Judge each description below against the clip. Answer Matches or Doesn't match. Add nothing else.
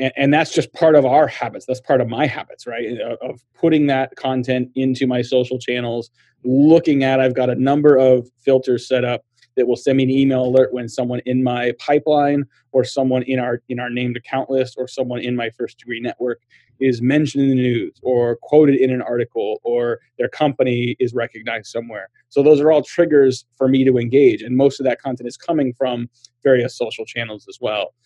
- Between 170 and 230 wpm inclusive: Matches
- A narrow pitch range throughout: Matches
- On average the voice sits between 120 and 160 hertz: Matches